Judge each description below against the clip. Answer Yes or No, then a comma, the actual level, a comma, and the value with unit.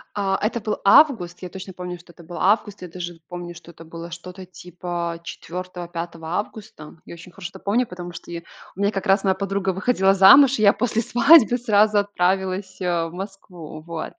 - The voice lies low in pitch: No, medium, 185 Hz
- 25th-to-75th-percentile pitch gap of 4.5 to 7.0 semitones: No, average, 2.8 semitones